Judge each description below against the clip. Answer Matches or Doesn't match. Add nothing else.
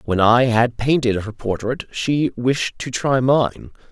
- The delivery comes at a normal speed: Matches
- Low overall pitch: Matches